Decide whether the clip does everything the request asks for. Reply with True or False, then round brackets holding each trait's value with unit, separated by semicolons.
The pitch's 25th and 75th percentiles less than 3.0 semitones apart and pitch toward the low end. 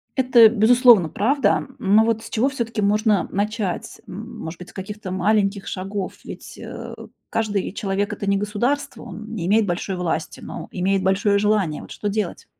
False (2.5 semitones; 205 Hz)